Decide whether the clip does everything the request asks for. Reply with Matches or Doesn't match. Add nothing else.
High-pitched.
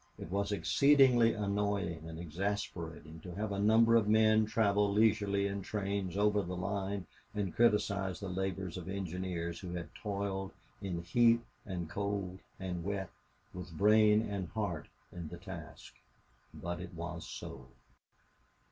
Doesn't match